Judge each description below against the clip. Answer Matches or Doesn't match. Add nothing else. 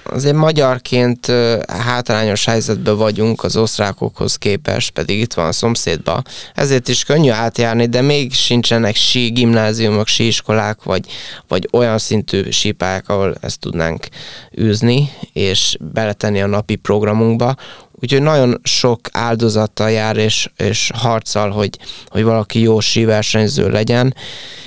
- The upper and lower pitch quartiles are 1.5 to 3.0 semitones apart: Matches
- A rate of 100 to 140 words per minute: Matches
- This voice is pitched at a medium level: Doesn't match